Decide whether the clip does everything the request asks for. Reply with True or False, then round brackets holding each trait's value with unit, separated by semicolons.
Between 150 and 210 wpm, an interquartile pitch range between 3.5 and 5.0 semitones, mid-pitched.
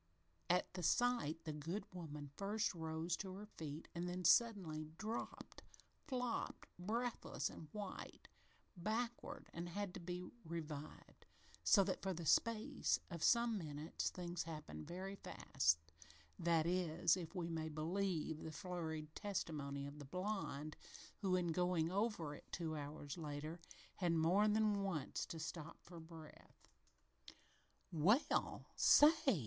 False (140 wpm; 4.0 semitones; 170 Hz)